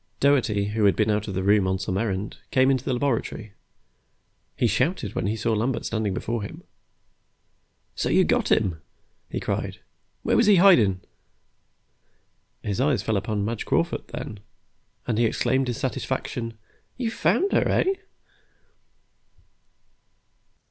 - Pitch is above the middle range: No, low, 110 Hz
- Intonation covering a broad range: No, average, 4.2 semitones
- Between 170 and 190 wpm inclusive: No, average, 145 wpm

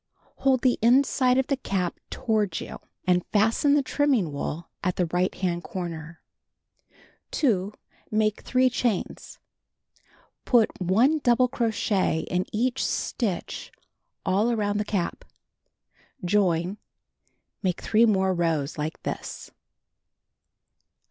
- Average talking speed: No, slow, 115 wpm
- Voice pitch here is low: No, high, 205 Hz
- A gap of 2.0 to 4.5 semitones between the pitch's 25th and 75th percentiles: No, average, 5.2 semitones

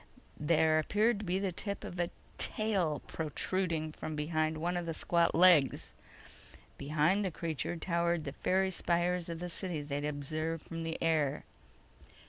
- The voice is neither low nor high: Yes, medium, 165 Hz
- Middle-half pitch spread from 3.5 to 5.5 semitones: No, narrow, 2.4 semitones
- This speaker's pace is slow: No, average, 155 wpm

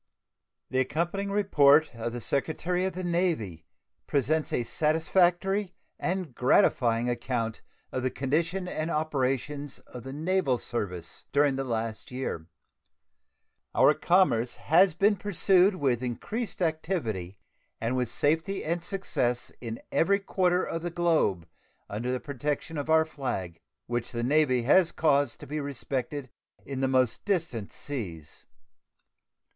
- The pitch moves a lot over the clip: Yes, wide, 6.1 semitones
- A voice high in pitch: No, medium, 145 Hz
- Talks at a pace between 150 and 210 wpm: No, slow, 135 wpm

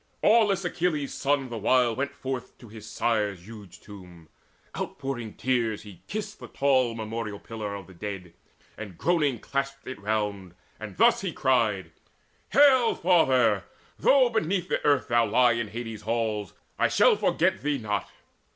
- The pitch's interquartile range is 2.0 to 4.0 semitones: No, average, 5.2 semitones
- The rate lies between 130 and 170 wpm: Yes, average, 155 wpm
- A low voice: Yes, low, 115 Hz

